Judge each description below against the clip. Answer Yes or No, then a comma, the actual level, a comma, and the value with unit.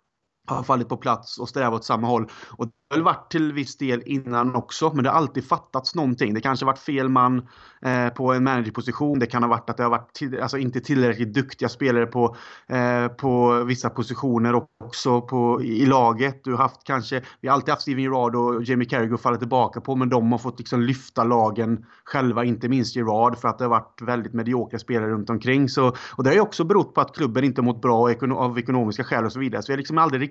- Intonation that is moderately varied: No, narrow, 1.9 semitones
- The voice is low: Yes, low, 125 Hz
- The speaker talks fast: Yes, fast, 240 wpm